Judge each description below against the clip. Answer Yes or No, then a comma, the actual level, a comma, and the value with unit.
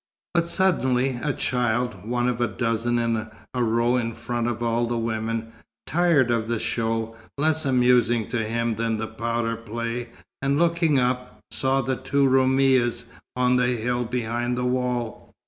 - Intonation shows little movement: Yes, narrow, 1.9 semitones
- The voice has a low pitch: Yes, low, 120 Hz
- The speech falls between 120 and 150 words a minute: No, average, 165 wpm